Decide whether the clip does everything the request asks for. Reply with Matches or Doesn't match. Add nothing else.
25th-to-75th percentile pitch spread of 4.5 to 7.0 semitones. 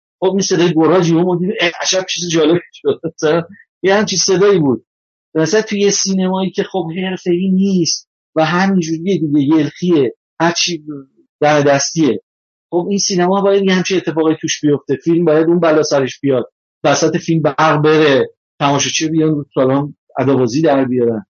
Doesn't match